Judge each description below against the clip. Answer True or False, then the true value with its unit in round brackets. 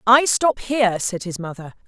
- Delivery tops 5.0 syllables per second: False (4.8 syllables/s)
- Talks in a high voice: True (210 Hz)